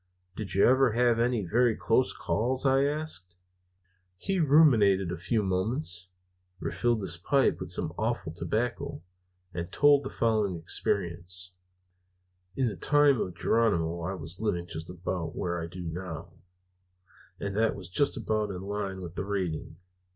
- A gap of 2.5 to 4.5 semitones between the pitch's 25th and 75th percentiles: No, wide, 5.4 semitones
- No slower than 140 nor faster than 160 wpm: Yes, average, 150 wpm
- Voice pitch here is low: Yes, low, 100 Hz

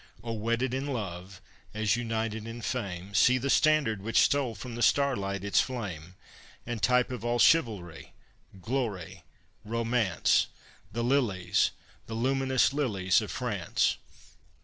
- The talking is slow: Yes, slow, 130 wpm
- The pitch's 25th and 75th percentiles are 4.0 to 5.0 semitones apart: Yes, average, 4.3 semitones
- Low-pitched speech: Yes, low, 115 Hz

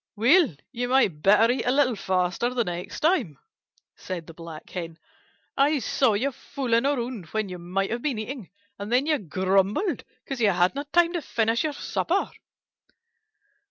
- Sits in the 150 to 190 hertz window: No, high, 230 Hz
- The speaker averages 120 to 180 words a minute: Yes, average, 165 wpm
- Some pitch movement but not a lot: No, wide, 6.5 semitones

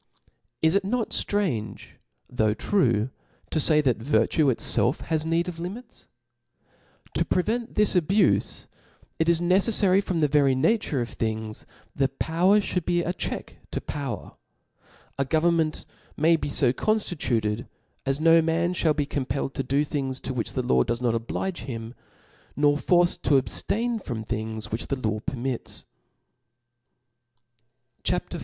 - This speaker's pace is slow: No, average, 150 wpm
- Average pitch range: No, wide, 6.0 semitones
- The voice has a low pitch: No, medium, 150 Hz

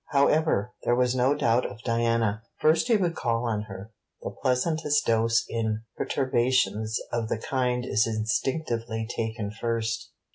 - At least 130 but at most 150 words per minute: Yes, average, 145 wpm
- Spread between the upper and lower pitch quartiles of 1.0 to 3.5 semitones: Yes, narrow, 2.6 semitones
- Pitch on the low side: Yes, low, 115 Hz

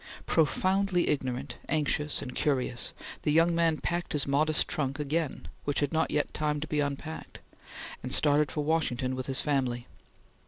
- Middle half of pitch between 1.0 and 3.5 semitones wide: Yes, narrow, 2.6 semitones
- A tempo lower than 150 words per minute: No, average, 160 wpm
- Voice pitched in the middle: Yes, medium, 150 Hz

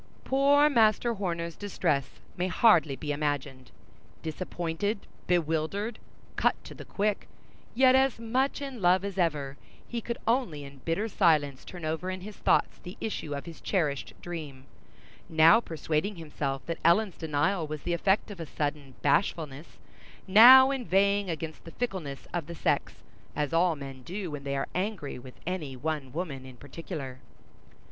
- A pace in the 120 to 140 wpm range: No, average, 155 wpm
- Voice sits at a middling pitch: Yes, medium, 170 Hz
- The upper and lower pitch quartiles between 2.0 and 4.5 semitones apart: No, wide, 5.5 semitones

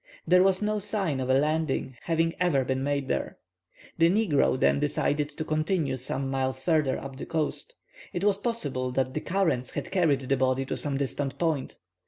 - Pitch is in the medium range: Yes, medium, 145 Hz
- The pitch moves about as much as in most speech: Yes, average, 4.5 semitones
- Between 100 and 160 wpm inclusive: No, average, 190 wpm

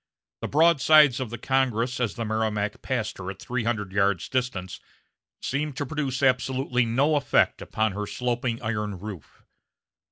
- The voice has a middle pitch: No, low, 120 Hz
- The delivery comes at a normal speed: Yes, average, 155 wpm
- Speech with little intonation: No, average, 3.9 semitones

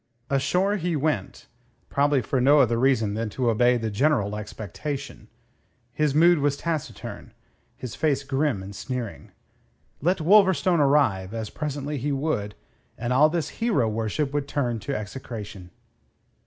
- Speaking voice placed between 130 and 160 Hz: Yes, low, 135 Hz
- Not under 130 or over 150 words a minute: Yes, average, 140 wpm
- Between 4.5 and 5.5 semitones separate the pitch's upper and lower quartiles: Yes, average, 5.1 semitones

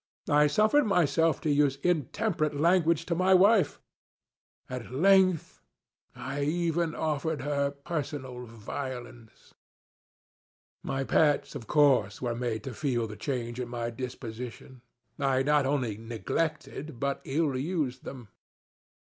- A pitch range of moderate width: Yes, average, 4.5 semitones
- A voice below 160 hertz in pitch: Yes, medium, 140 Hz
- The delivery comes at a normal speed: No, slow, 120 wpm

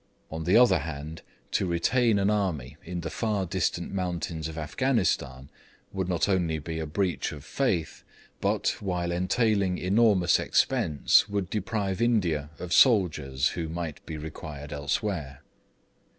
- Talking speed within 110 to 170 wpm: Yes, average, 140 wpm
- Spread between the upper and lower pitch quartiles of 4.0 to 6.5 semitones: Yes, average, 4.4 semitones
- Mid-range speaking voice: No, very low, 85 Hz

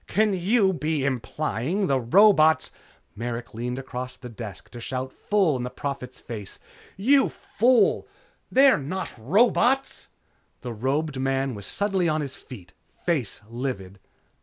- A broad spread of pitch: Yes, wide, 7.6 semitones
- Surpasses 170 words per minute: No, average, 145 wpm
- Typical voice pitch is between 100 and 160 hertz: Yes, low, 135 Hz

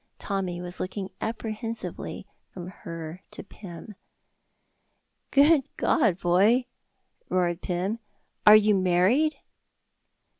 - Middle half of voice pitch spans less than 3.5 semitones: No, average, 4.0 semitones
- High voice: Yes, high, 195 Hz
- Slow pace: Yes, slow, 90 wpm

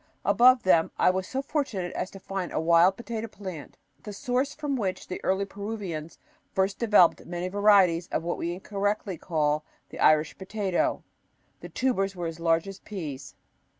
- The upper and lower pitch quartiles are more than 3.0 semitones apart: Yes, average, 3.7 semitones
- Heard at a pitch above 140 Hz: Yes, high, 190 Hz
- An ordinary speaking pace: Yes, average, 170 wpm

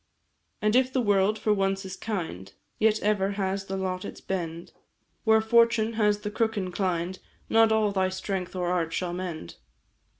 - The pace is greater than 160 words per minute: Yes, average, 170 wpm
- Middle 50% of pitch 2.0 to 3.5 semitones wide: Yes, average, 3.0 semitones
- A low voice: No, high, 195 Hz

